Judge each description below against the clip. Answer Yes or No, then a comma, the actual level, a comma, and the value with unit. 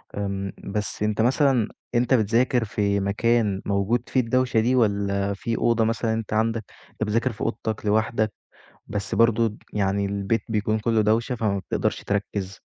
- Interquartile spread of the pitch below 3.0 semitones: Yes, narrow, 2.4 semitones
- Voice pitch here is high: No, low, 110 Hz